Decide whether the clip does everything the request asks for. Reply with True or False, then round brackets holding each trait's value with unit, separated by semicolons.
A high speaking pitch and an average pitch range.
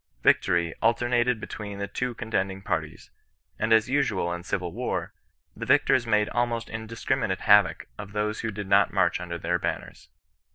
False (105 Hz; 3.4 semitones)